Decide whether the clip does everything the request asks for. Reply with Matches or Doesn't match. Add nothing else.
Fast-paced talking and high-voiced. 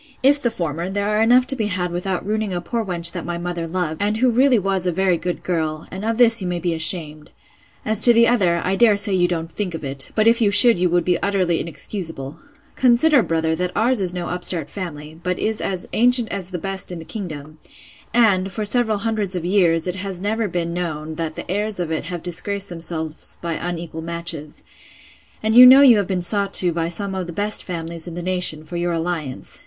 Doesn't match